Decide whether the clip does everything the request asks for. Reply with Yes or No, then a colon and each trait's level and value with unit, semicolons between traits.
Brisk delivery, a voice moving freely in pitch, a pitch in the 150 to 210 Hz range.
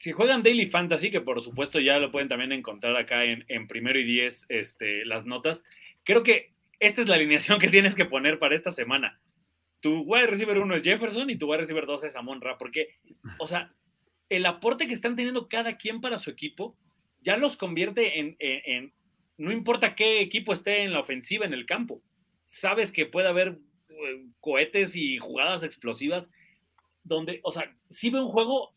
Yes: fast, 195 wpm; wide, 7.1 semitones; medium, 185 Hz